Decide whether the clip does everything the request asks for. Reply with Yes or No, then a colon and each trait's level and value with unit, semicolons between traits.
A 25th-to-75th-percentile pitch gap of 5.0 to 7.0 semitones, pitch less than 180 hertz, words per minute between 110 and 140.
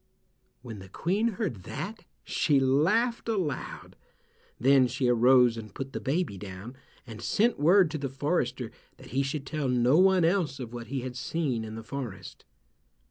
No: wide, 5.6 semitones; low, 135 Hz; average, 170 wpm